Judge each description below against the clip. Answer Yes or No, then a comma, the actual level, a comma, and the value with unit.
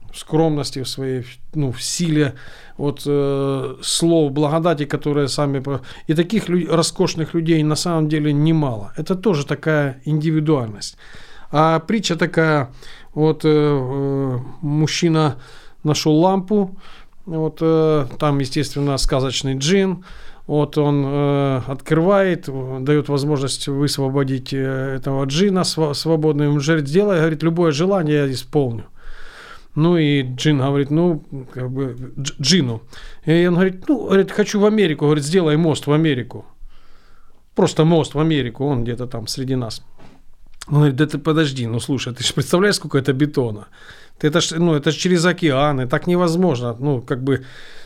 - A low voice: No, medium, 150 Hz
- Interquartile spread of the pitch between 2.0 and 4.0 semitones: Yes, average, 3.1 semitones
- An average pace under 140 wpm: No, average, 145 wpm